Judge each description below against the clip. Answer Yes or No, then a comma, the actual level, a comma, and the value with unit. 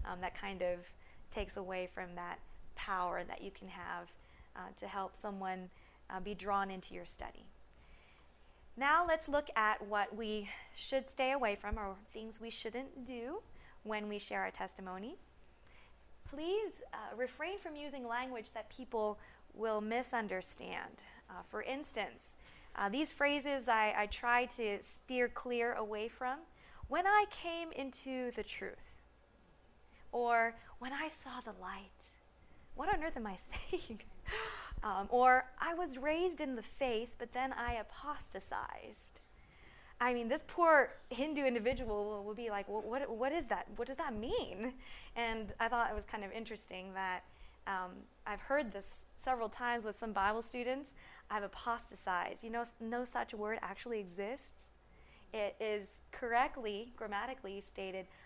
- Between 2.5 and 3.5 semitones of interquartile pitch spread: No, average, 4.1 semitones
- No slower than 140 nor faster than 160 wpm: Yes, average, 150 wpm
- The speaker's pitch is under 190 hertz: No, high, 230 Hz